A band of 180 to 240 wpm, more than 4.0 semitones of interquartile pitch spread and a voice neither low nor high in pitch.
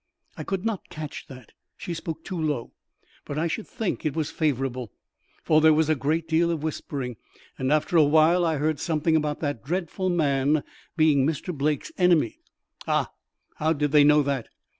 No: average, 185 wpm; narrow, 2.4 semitones; medium, 155 Hz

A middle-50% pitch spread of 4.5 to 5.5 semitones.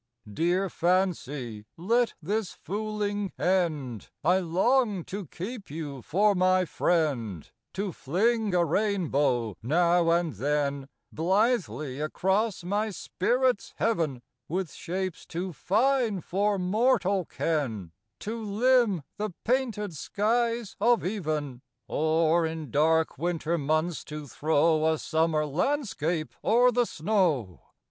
Yes: average, 5.2 semitones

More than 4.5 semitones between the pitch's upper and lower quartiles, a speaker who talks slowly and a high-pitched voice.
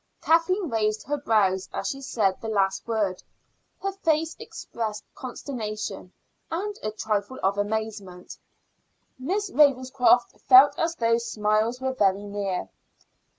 Yes: average, 5.2 semitones; slow, 125 wpm; high, 225 Hz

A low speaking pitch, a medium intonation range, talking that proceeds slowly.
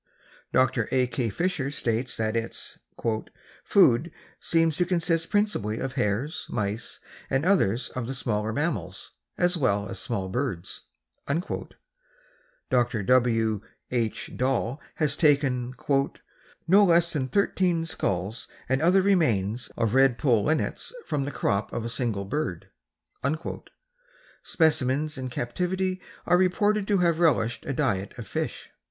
No: low, 130 Hz; wide, 6.7 semitones; slow, 130 wpm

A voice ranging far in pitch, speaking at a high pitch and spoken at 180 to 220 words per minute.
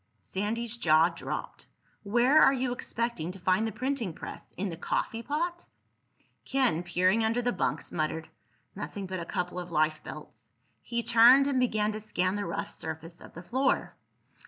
No: wide, 5.7 semitones; high, 210 Hz; average, 165 wpm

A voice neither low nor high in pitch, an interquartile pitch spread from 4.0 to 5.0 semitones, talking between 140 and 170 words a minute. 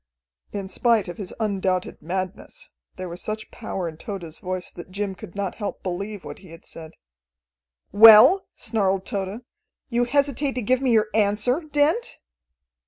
No: high, 205 Hz; average, 4.4 semitones; average, 160 wpm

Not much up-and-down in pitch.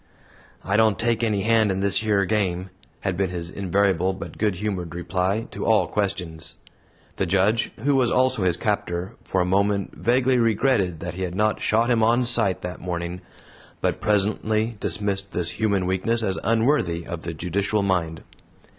No: average, 3.5 semitones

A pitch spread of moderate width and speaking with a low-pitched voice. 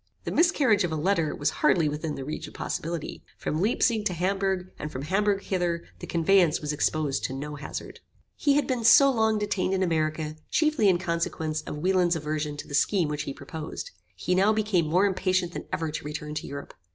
No: average, 4.5 semitones; medium, 170 Hz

